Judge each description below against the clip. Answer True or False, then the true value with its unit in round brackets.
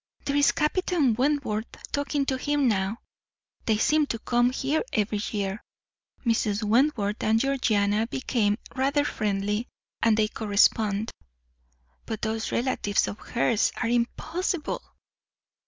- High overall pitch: True (230 Hz)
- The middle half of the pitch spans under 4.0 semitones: False (4.6 semitones)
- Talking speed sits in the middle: False (120 wpm)